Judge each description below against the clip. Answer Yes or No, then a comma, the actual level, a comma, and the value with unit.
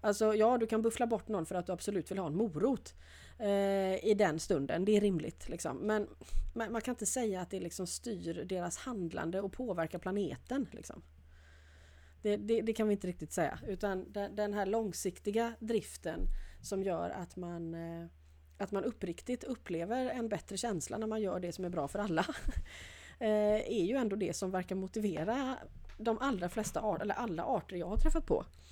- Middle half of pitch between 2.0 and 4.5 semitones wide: Yes, average, 4.2 semitones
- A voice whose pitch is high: Yes, high, 200 Hz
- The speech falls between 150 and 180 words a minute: No, average, 190 wpm